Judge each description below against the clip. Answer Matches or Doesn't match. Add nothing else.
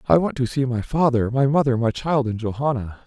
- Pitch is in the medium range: Doesn't match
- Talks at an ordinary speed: Doesn't match